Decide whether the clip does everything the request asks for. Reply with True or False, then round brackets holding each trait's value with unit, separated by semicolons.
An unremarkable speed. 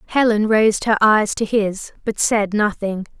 True (170 wpm)